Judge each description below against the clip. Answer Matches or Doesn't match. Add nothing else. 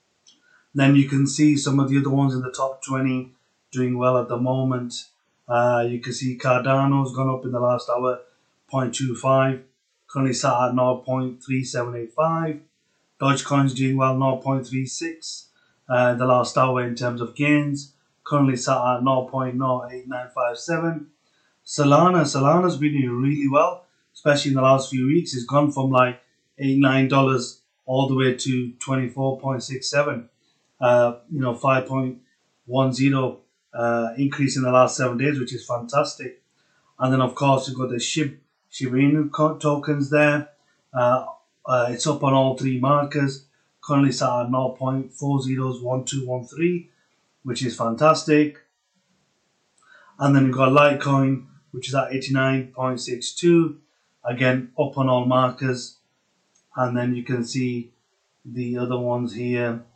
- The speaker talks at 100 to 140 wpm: Matches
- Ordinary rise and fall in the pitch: Doesn't match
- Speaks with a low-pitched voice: Matches